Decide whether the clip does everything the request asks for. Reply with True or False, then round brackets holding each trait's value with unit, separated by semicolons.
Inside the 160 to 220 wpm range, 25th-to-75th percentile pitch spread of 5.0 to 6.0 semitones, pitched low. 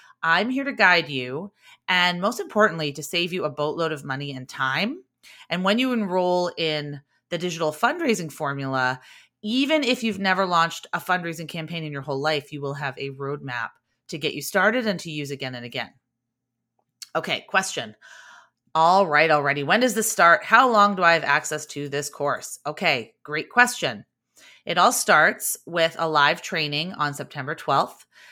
False (180 wpm; 5.3 semitones; 165 Hz)